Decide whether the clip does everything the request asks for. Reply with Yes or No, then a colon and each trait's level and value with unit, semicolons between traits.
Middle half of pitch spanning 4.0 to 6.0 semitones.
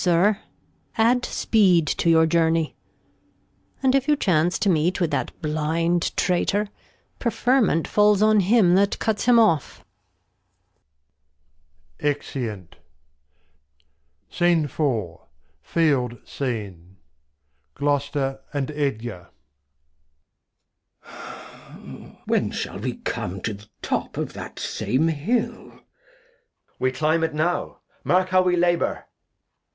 Yes: average, 5.2 semitones